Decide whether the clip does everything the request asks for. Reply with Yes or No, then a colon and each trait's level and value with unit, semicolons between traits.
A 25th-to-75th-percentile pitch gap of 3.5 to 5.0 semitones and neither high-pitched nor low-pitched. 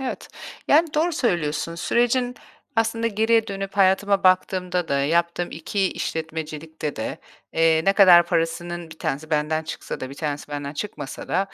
Yes: average, 4.2 semitones; medium, 175 Hz